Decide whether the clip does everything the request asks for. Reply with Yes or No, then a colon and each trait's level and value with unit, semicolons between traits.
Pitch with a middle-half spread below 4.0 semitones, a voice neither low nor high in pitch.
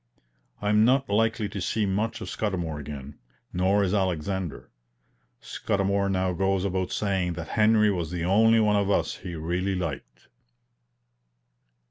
No: average, 2.9 semitones; very low, 95 Hz